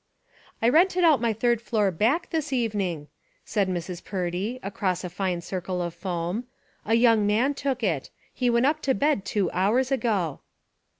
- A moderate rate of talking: Yes, average, 175 wpm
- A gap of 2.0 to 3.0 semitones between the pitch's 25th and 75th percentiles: No, wide, 5.6 semitones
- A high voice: Yes, high, 210 Hz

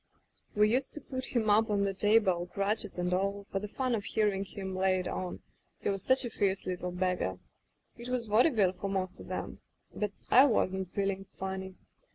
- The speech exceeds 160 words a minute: Yes, fast, 205 wpm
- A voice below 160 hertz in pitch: No, high, 200 Hz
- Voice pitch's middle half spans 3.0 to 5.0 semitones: No, narrow, 2.5 semitones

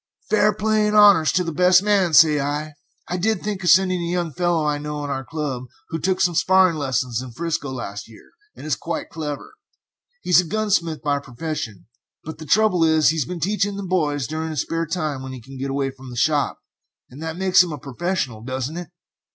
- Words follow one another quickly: Yes, fast, 220 wpm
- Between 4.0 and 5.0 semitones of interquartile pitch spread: Yes, average, 4.5 semitones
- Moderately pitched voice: Yes, medium, 160 Hz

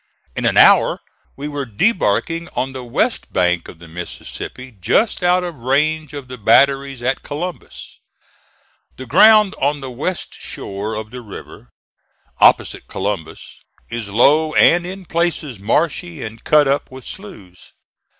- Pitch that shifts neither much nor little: No, wide, 6.9 semitones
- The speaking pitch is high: No, low, 135 Hz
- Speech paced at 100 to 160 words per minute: Yes, average, 145 wpm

